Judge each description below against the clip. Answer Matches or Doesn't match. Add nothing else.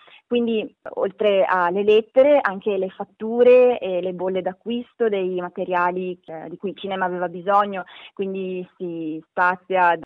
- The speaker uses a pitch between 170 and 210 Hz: Matches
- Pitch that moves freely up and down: Doesn't match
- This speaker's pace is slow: Doesn't match